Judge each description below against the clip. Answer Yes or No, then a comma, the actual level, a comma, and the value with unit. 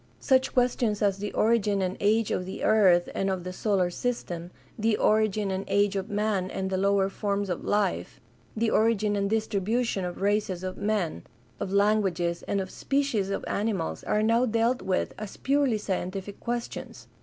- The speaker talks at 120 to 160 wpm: No, average, 180 wpm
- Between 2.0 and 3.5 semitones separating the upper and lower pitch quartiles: Yes, narrow, 2.6 semitones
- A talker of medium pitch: No, high, 205 Hz